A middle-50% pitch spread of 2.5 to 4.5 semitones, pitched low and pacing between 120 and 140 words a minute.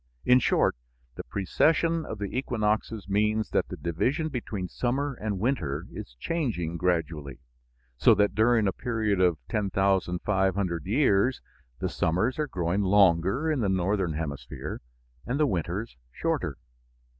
No: average, 5.3 semitones; low, 100 Hz; slow, 135 wpm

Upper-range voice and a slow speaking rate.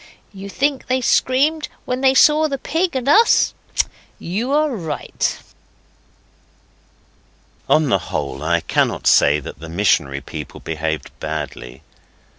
Yes: high, 230 Hz; slow, 125 wpm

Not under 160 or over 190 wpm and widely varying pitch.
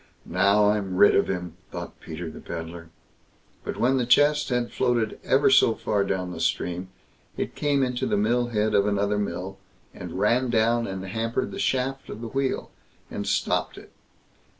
No: average, 175 wpm; average, 4.5 semitones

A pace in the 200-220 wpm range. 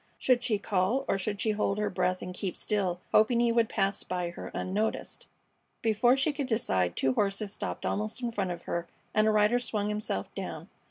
Yes: fast, 205 wpm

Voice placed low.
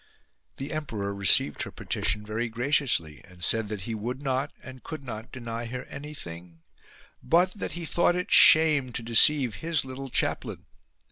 Yes: low, 125 Hz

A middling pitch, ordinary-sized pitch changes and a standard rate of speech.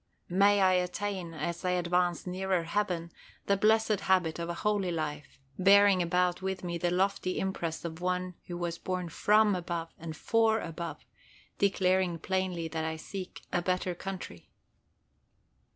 No: medium, 180 Hz; narrow, 2.1 semitones; average, 150 wpm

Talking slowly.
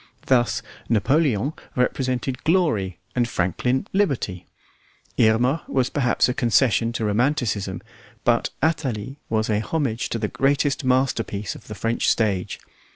Yes: slow, 125 wpm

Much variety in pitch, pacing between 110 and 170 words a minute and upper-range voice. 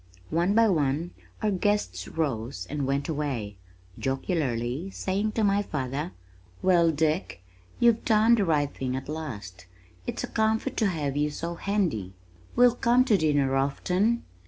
No: wide, 7.0 semitones; average, 150 wpm; medium, 160 Hz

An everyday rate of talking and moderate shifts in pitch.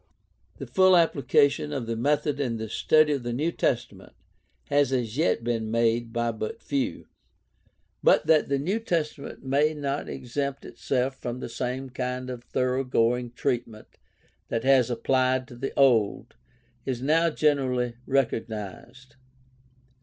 Yes: average, 145 wpm; average, 3.0 semitones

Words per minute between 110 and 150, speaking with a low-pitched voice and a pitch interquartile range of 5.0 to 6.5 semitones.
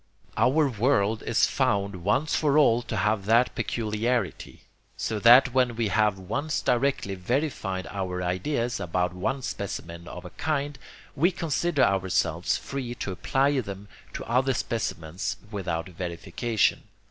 Yes: slow, 135 wpm; low, 110 Hz; wide, 5.6 semitones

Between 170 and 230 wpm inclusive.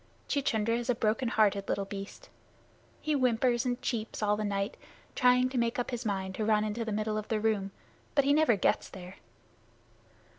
Yes: average, 190 wpm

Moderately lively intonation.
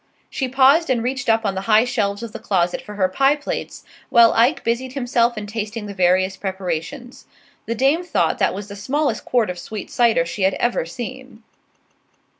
Yes: average, 4.3 semitones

